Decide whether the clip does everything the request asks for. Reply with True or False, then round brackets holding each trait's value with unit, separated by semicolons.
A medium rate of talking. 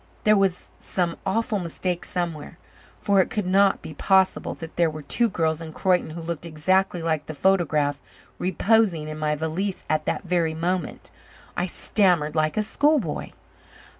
True (165 wpm)